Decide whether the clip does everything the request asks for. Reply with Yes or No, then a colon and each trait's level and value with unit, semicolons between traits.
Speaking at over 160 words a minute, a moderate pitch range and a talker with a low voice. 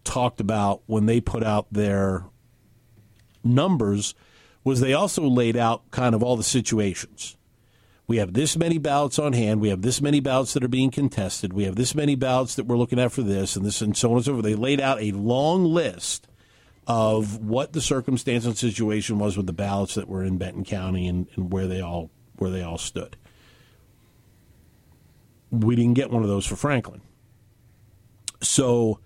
Yes: average, 190 wpm; average, 3.7 semitones; low, 115 Hz